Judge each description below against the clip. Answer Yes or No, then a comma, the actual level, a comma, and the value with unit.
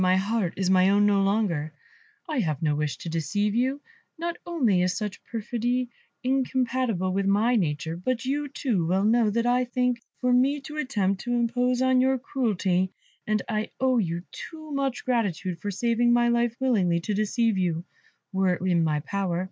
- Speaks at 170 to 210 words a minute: Yes, average, 180 wpm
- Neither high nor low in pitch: No, high, 220 Hz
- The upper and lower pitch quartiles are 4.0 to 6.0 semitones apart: Yes, average, 5.1 semitones